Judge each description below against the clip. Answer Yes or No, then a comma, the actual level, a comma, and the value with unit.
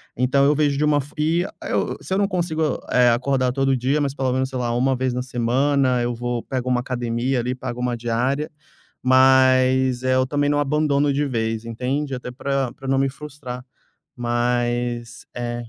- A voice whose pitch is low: Yes, low, 130 Hz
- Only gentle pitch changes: Yes, narrow, 2.3 semitones